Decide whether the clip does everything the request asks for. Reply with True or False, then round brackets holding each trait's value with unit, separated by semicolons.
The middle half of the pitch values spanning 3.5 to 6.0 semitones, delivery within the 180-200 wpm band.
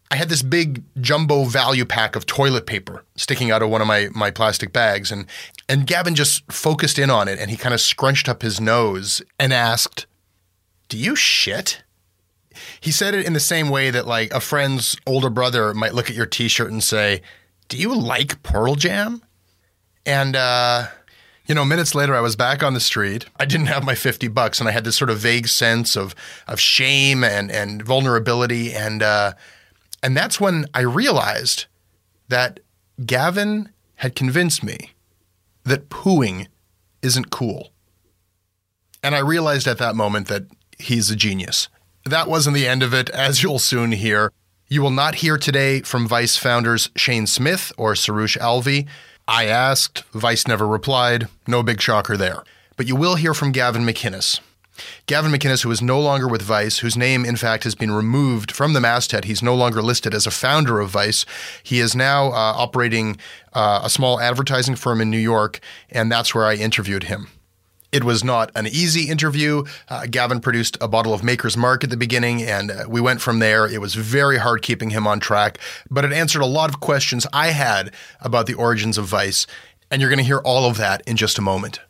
True (4.1 semitones; 195 wpm)